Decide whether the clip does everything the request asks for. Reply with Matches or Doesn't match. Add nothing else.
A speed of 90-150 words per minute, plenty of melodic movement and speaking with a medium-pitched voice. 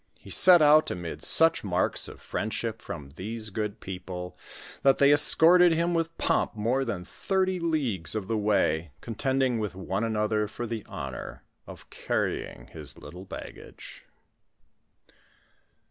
Doesn't match